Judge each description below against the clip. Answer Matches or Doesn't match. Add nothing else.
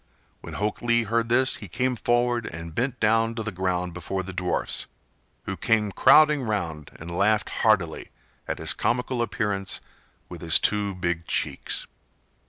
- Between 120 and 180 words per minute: Matches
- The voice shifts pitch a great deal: Doesn't match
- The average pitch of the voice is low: Matches